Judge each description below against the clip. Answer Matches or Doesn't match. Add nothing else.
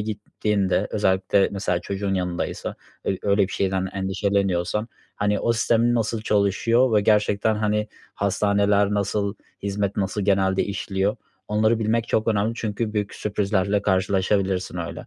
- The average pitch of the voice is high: Doesn't match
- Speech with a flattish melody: Matches